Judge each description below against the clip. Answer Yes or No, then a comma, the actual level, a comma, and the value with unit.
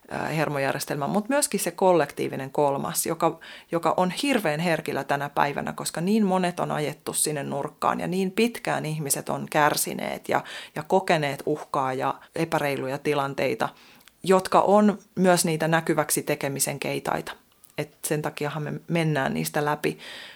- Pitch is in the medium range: Yes, medium, 160 Hz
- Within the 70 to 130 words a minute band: No, average, 140 wpm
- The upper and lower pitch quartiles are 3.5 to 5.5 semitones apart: Yes, average, 4.2 semitones